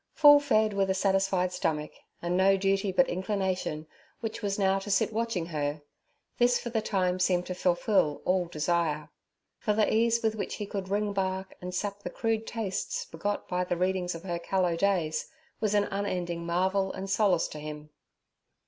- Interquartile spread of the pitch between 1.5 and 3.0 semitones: Yes, average, 2.7 semitones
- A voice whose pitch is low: No, high, 190 Hz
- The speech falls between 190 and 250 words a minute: No, average, 180 wpm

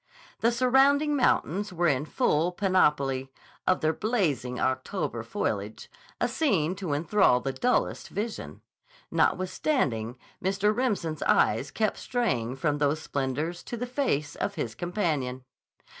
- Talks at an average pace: No, slow, 130 wpm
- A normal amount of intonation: No, wide, 8.0 semitones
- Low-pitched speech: No, medium, 170 Hz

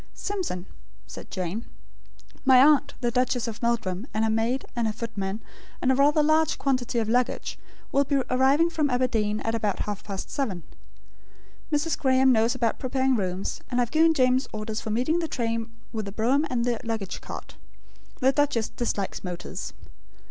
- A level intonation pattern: No, average, 3.6 semitones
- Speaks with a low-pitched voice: No, high, 240 Hz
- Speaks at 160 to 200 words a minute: Yes, average, 175 wpm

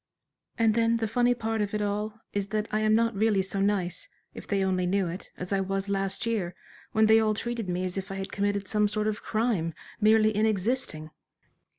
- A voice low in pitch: No, high, 210 Hz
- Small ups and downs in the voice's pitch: Yes, narrow, 2.2 semitones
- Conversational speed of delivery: No, fast, 220 wpm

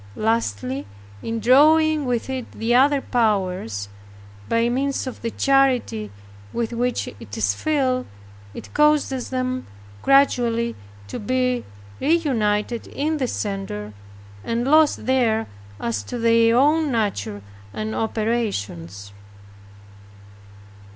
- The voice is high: Yes, high, 235 Hz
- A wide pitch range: No, average, 4.1 semitones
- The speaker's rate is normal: No, slow, 110 wpm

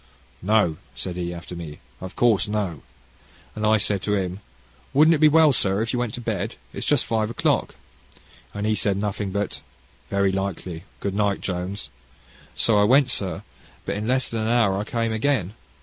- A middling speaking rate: Yes, average, 185 wpm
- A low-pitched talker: Yes, low, 105 Hz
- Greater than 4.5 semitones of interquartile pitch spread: No, average, 3.1 semitones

